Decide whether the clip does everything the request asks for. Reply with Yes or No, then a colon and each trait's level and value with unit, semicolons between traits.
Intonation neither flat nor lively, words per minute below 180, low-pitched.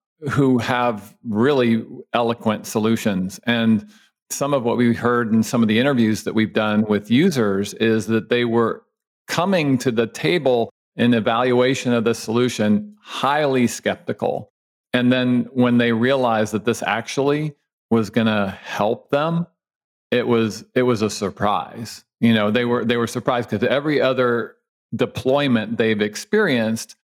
No: narrow, 2.1 semitones; average, 150 wpm; low, 120 Hz